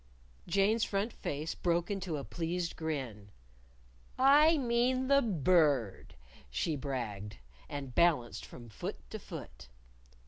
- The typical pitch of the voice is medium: Yes, medium, 165 Hz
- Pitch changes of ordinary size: No, wide, 8.5 semitones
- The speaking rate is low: Yes, slow, 125 wpm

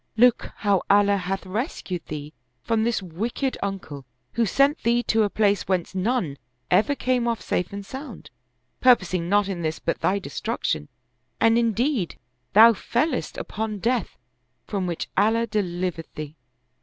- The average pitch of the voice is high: Yes, high, 205 Hz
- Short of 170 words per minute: Yes, average, 150 wpm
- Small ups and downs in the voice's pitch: No, average, 4.2 semitones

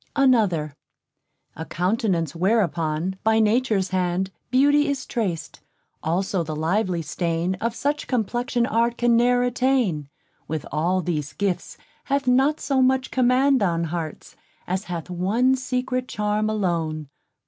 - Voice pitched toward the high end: Yes, high, 210 Hz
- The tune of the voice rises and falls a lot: Yes, wide, 6.5 semitones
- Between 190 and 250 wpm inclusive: No, slow, 135 wpm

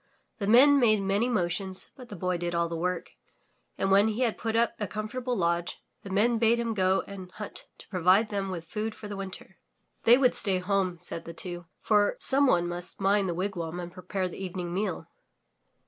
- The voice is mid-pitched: No, high, 195 Hz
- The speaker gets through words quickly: Yes, fast, 210 wpm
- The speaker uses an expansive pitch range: No, average, 3.3 semitones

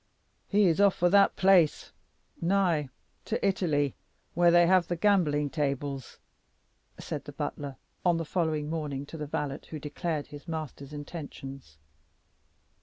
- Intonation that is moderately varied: Yes, average, 3.3 semitones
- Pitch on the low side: No, medium, 160 Hz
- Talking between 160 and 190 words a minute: No, average, 140 wpm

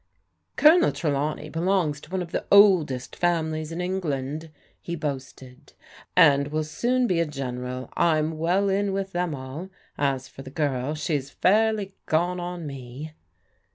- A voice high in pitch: No, medium, 155 Hz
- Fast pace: No, average, 170 wpm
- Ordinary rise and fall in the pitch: Yes, average, 4.4 semitones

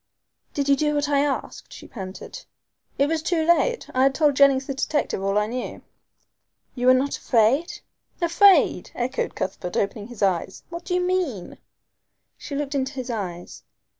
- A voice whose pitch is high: Yes, very high, 275 Hz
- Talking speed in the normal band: Yes, average, 170 wpm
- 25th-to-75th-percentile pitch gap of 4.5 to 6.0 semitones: Yes, average, 4.9 semitones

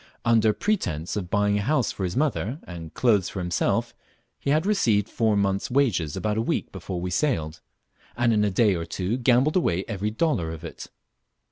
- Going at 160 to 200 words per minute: Yes, average, 195 wpm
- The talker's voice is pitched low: Yes, low, 105 Hz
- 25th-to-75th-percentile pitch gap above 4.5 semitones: Yes, average, 5.2 semitones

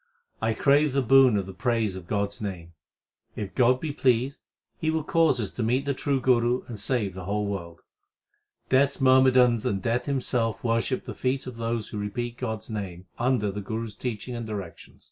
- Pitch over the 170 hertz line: No, low, 115 Hz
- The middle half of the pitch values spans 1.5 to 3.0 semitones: No, average, 4.0 semitones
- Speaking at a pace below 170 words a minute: No, fast, 205 wpm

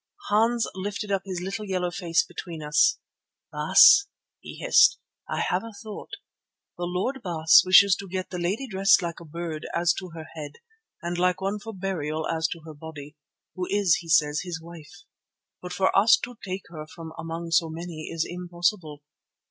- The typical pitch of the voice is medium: Yes, medium, 175 Hz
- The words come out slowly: No, average, 180 wpm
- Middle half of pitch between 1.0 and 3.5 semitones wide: Yes, average, 3.2 semitones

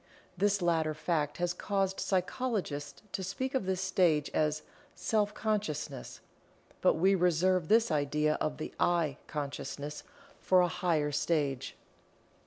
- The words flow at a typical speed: No, slow, 130 wpm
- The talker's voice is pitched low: No, medium, 175 Hz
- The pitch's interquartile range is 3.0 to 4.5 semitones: Yes, average, 4.1 semitones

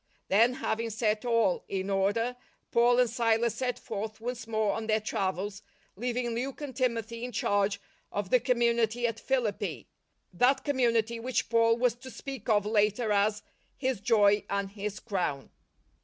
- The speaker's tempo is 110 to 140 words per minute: No, average, 165 wpm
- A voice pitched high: Yes, high, 230 Hz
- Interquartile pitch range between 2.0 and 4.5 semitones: Yes, average, 2.8 semitones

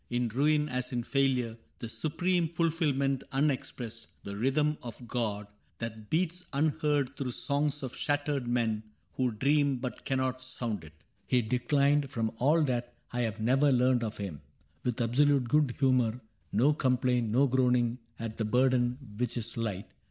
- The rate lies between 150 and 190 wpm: Yes, average, 160 wpm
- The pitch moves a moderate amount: Yes, average, 3.3 semitones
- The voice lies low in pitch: Yes, low, 125 Hz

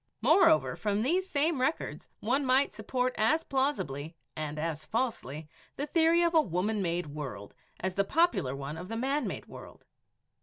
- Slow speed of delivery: No, average, 165 wpm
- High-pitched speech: Yes, high, 225 Hz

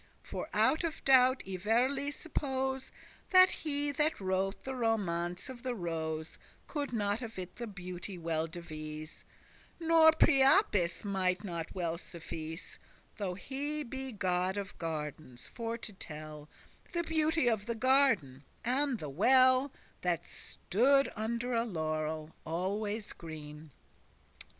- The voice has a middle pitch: No, high, 205 Hz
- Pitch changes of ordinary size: No, wide, 7.8 semitones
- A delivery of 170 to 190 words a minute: No, average, 140 wpm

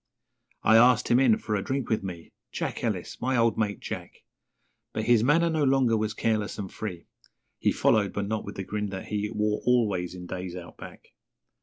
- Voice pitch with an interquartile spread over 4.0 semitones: No, average, 3.2 semitones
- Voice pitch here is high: No, low, 110 Hz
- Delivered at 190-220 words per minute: Yes, average, 200 wpm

